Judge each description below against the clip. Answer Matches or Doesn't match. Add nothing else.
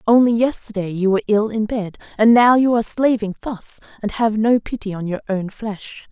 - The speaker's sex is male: Doesn't match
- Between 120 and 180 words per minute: Doesn't match